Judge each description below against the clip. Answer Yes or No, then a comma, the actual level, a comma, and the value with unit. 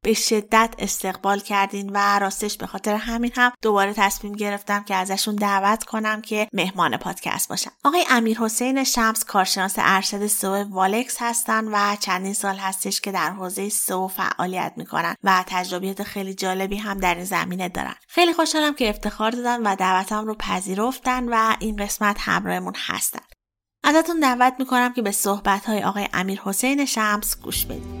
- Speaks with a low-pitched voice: No, high, 205 Hz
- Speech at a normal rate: No, fast, 165 wpm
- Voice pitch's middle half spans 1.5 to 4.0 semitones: Yes, average, 2.7 semitones